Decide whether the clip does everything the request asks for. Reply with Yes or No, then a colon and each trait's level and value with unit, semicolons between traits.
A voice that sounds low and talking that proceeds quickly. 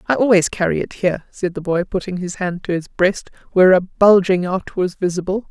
No: medium, 185 Hz; fast, 220 wpm